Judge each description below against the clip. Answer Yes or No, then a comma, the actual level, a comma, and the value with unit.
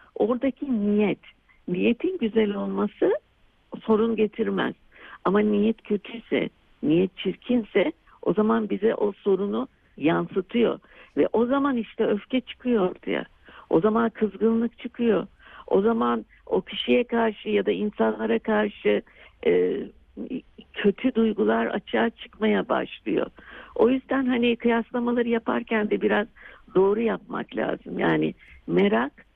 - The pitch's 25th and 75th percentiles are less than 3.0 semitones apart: Yes, narrow, 2.4 semitones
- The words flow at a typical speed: Yes, average, 115 wpm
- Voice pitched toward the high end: Yes, high, 225 Hz